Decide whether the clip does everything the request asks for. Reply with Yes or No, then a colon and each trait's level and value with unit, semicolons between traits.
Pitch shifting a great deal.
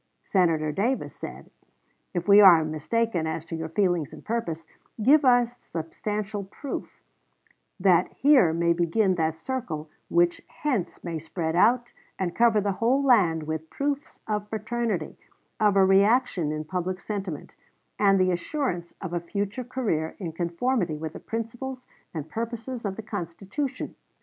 Yes: wide, 5.7 semitones